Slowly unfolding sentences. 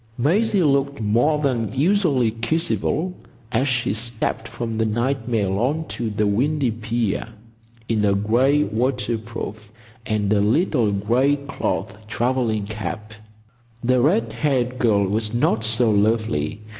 Yes: slow, 130 wpm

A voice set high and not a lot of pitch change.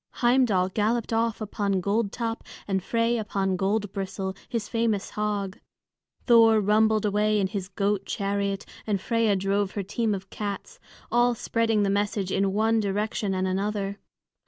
Yes: high, 205 Hz; narrow, 2.3 semitones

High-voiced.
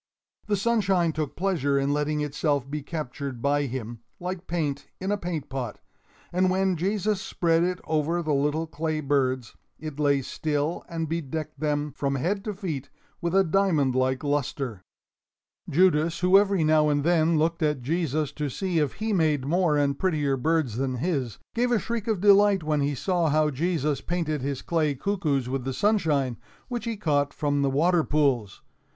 No: medium, 155 Hz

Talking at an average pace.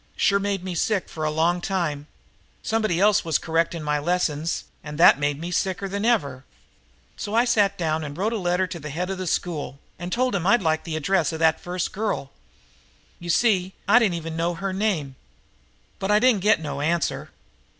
No: fast, 210 wpm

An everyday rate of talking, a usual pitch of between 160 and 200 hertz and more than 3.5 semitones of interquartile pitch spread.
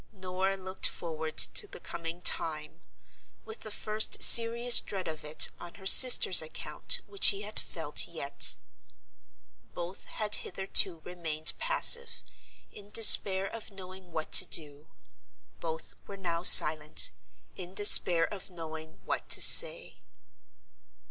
No: slow, 130 wpm; medium, 185 Hz; average, 4.2 semitones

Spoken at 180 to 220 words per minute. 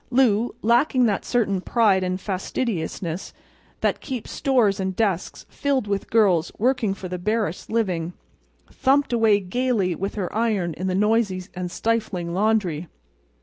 No: average, 145 wpm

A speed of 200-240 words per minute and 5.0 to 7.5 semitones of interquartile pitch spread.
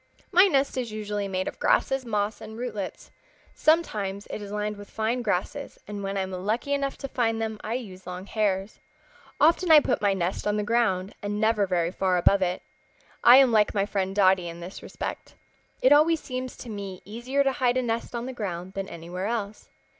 No: fast, 205 wpm; average, 4.2 semitones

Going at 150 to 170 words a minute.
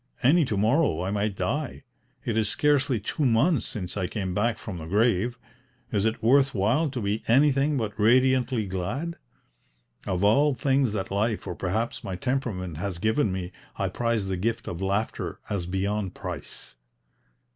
Yes: average, 165 wpm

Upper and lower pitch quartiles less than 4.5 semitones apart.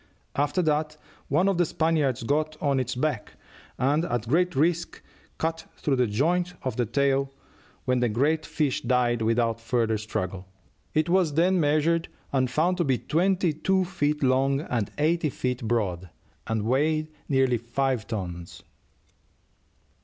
No: average, 4.9 semitones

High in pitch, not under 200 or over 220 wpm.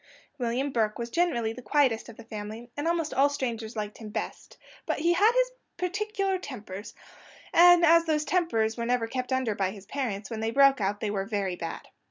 Yes: high, 240 Hz; fast, 205 wpm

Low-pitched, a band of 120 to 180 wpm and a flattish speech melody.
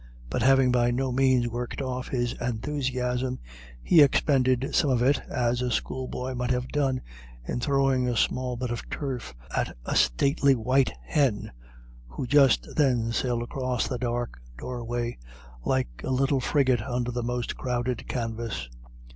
Yes: low, 125 Hz; average, 155 wpm; narrow, 1.6 semitones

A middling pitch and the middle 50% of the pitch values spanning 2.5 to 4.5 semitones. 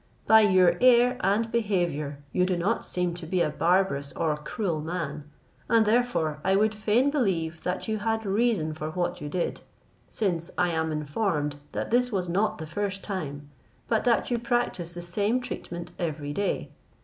No: medium, 180 Hz; average, 5.3 semitones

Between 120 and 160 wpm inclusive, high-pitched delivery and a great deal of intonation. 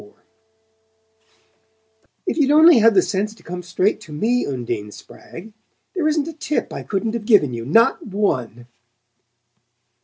Yes: average, 150 wpm; high, 210 Hz; wide, 8.1 semitones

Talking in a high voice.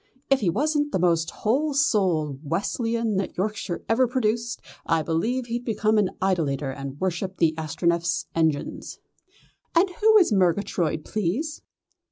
Yes: high, 195 Hz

